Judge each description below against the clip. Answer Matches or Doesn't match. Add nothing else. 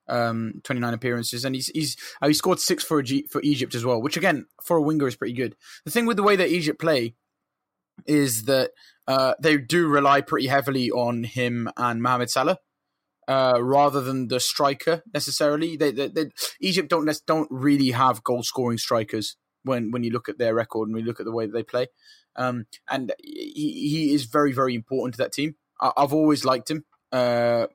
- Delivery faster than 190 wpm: Matches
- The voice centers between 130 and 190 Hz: Matches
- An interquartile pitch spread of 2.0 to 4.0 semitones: Matches